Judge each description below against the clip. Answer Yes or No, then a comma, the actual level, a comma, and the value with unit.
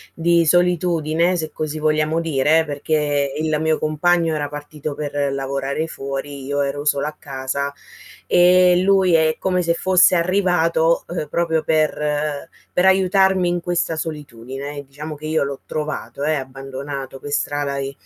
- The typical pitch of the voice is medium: Yes, medium, 155 Hz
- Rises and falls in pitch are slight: No, average, 3.0 semitones